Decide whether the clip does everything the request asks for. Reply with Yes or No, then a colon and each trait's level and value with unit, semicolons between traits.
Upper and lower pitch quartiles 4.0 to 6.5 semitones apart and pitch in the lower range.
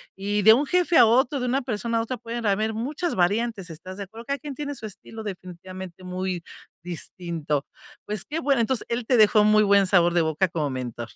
No: average, 4.8 semitones; high, 210 Hz